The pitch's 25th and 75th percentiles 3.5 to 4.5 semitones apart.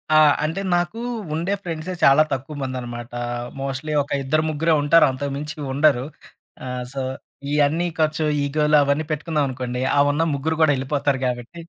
No: narrow, 2.6 semitones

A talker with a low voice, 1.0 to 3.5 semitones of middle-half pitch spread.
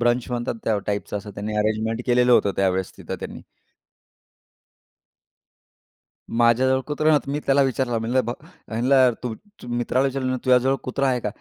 Yes: low, 125 Hz; average, 2.9 semitones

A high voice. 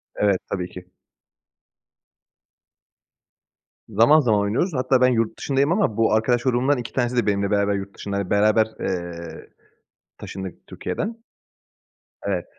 No: low, 110 Hz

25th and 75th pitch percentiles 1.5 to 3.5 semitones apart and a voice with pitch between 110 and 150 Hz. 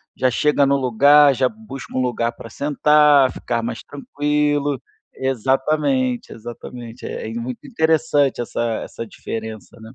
No: average, 3.9 semitones; low, 135 Hz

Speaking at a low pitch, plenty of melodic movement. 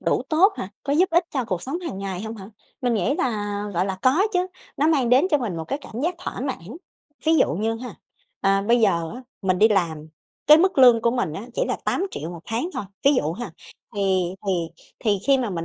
No: high, 230 Hz; wide, 6.5 semitones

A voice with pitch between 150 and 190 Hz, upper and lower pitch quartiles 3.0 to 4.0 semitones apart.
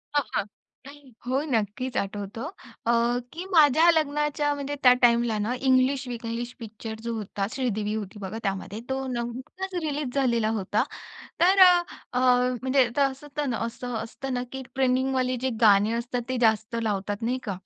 No: high, 245 Hz; average, 3.6 semitones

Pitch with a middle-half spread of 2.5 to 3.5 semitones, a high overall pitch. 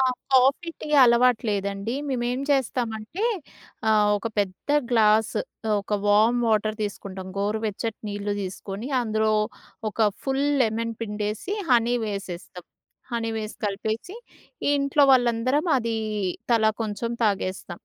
Yes: average, 2.9 semitones; high, 220 Hz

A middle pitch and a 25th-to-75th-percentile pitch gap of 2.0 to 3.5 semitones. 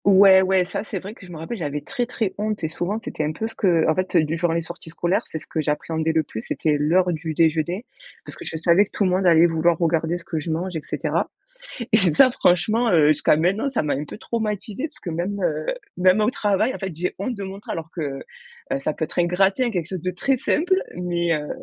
No: medium, 175 Hz; average, 3.9 semitones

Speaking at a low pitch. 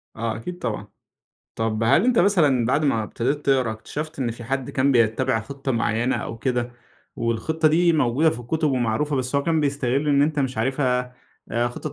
Yes: low, 130 Hz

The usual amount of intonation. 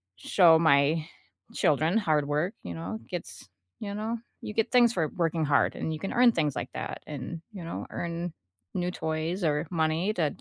Yes: average, 3.5 semitones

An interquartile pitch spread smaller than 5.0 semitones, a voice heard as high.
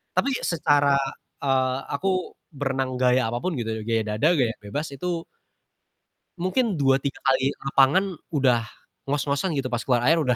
No: average, 2.8 semitones; low, 135 Hz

